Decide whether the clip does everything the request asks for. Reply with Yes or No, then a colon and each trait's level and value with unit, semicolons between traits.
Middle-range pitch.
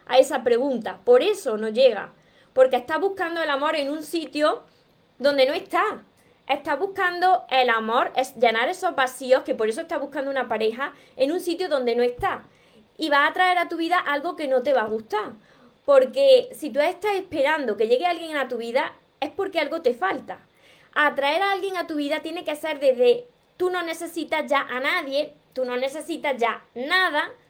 No: very high, 295 Hz